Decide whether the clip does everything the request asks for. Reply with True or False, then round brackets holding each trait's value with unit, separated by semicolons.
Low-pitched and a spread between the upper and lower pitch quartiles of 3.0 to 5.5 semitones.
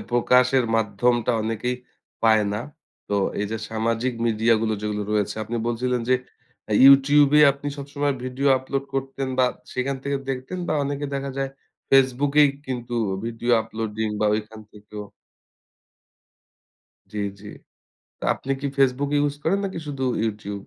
True (125 Hz; 3.7 semitones)